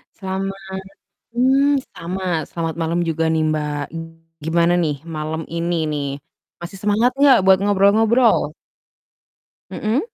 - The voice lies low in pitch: No, high, 190 Hz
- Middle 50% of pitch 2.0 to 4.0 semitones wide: No, average, 5.1 semitones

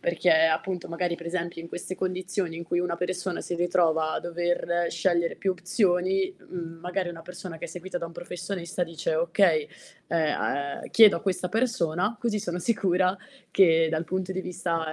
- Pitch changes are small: Yes, narrow, 1.8 semitones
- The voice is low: No, medium, 175 Hz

